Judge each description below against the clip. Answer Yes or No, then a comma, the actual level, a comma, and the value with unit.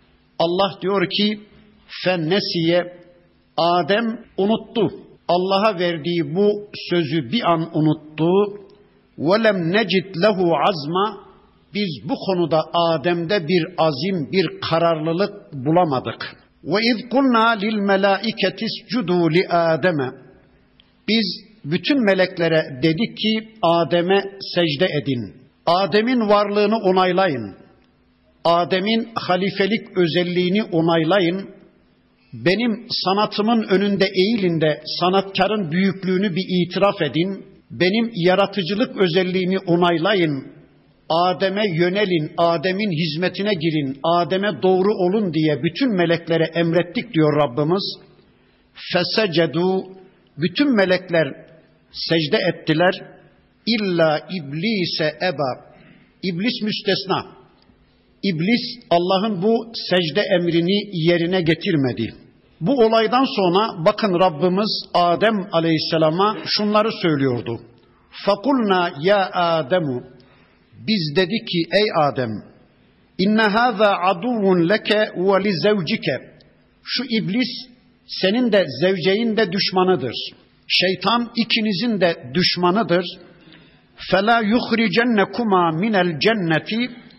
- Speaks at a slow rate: Yes, slow, 90 wpm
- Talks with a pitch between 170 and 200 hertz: Yes, medium, 185 Hz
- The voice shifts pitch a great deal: No, average, 3.7 semitones